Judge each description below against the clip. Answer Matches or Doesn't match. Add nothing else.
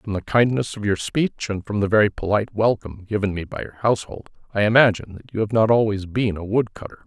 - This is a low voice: Matches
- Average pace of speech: Doesn't match